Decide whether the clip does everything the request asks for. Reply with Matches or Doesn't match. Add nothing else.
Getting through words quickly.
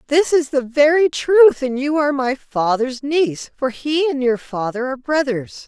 Doesn't match